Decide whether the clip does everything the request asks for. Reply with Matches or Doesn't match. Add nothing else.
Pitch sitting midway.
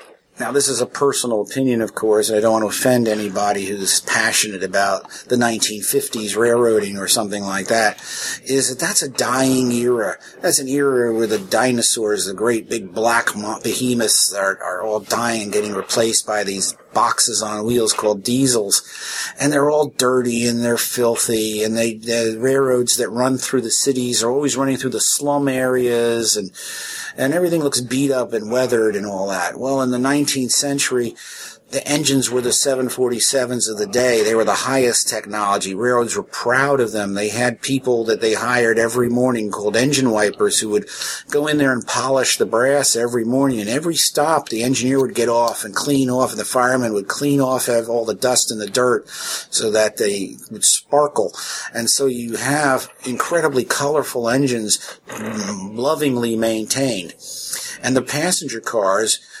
Doesn't match